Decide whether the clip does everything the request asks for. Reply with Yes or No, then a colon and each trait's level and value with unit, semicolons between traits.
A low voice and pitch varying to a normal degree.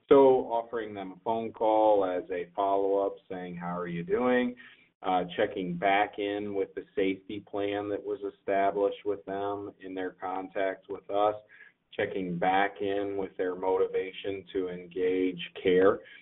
No: low, 100 Hz; narrow, 1.8 semitones